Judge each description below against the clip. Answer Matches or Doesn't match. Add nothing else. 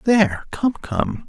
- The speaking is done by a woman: Doesn't match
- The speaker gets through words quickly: Doesn't match